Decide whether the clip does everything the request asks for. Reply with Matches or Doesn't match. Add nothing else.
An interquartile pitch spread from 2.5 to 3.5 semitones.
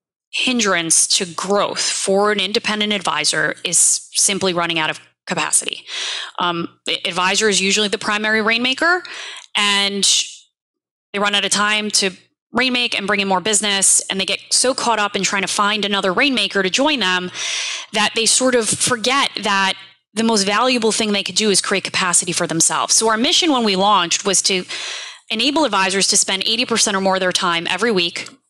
Matches